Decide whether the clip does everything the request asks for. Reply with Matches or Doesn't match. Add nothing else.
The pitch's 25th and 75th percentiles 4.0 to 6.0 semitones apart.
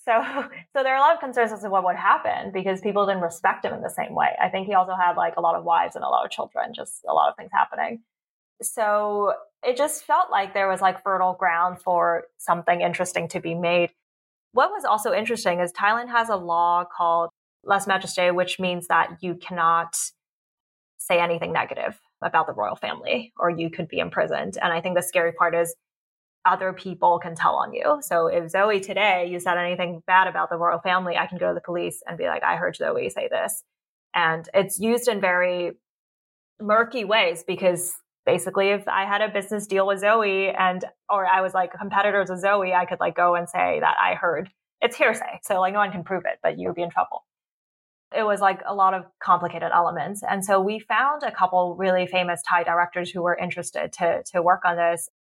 Doesn't match